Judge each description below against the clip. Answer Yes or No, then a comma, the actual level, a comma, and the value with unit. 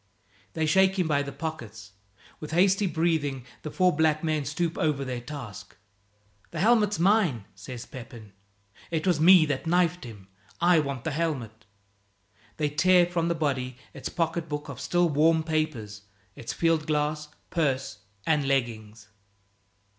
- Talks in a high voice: No, medium, 155 Hz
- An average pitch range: Yes, average, 4.6 semitones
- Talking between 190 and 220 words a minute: No, average, 150 wpm